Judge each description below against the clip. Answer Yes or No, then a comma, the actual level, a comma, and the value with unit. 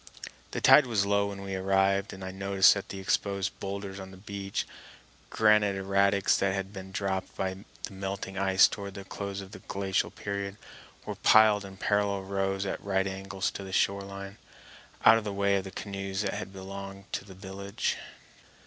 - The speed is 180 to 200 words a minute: Yes, average, 185 wpm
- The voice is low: Yes, low, 100 Hz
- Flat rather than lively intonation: Yes, narrow, 0.6 semitones